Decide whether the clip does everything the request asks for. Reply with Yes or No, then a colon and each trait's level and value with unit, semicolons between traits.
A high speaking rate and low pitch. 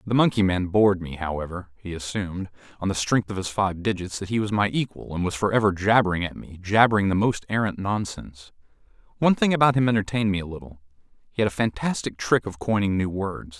Yes: fast, 210 wpm; low, 100 Hz